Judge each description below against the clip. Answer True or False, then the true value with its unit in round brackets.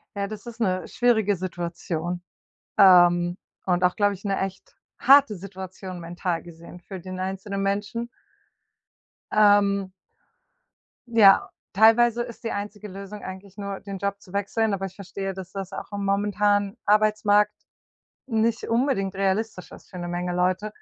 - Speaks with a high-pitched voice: True (195 Hz)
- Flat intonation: True (2.2 semitones)